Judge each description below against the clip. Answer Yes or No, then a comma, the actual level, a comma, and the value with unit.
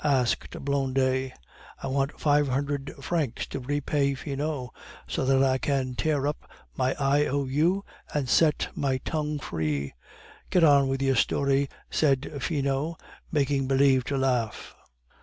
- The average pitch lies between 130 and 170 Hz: Yes, medium, 140 Hz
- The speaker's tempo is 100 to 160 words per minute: Yes, average, 140 wpm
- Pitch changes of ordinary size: No, narrow, 1.8 semitones